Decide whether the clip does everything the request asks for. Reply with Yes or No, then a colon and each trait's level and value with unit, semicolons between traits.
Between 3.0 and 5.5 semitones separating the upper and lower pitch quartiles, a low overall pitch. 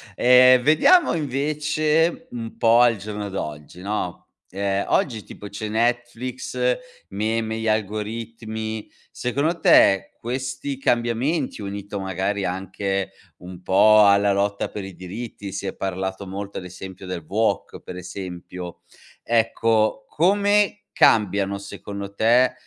Yes: average, 3.8 semitones; low, 105 Hz